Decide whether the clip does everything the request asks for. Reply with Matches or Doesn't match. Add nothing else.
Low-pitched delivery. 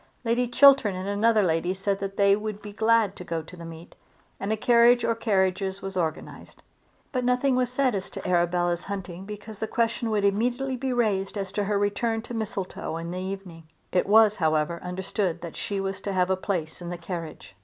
Doesn't match